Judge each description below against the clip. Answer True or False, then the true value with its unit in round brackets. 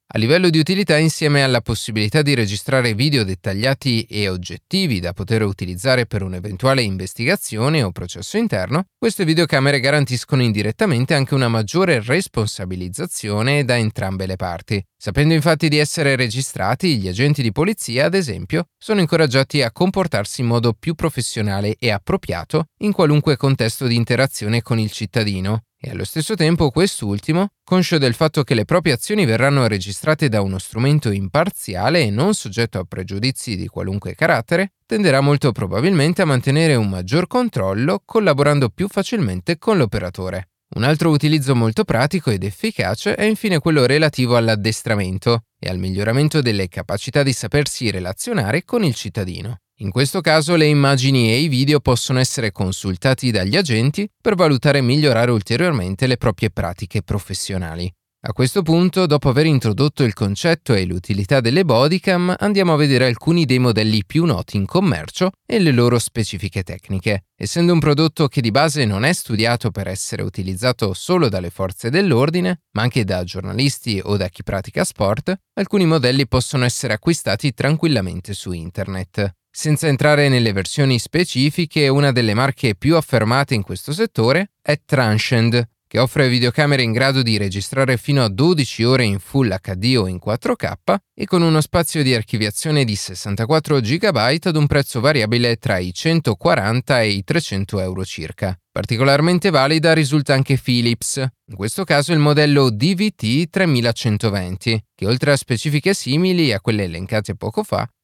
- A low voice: True (130 Hz)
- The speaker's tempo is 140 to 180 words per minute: True (155 wpm)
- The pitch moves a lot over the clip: True (6.5 semitones)